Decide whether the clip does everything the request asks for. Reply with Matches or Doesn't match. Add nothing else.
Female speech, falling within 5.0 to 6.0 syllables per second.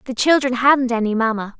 Matches